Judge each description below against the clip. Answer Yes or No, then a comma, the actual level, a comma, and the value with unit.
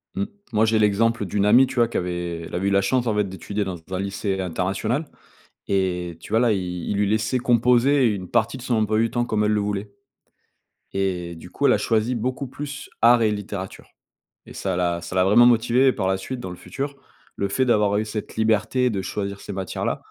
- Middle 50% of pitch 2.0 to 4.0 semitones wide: Yes, average, 3.7 semitones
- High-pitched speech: No, low, 105 Hz